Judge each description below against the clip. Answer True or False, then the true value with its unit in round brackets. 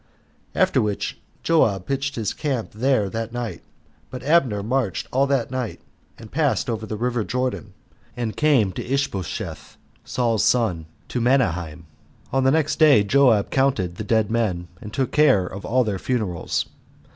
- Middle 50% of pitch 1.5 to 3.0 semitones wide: False (4.6 semitones)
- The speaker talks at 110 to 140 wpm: False (155 wpm)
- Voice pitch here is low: True (115 Hz)